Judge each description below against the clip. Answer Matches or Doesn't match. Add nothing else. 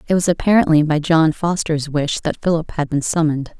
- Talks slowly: Doesn't match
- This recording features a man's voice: Doesn't match